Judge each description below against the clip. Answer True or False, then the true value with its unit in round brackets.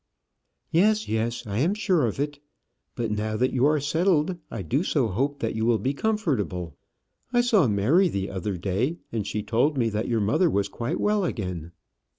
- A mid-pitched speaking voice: False (120 Hz)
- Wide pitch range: True (7.4 semitones)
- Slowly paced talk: False (190 wpm)